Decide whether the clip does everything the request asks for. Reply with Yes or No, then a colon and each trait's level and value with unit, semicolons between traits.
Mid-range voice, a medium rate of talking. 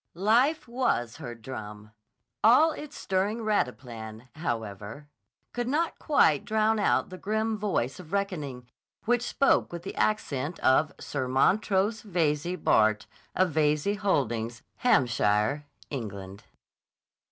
No: medium, 155 Hz; slow, 120 wpm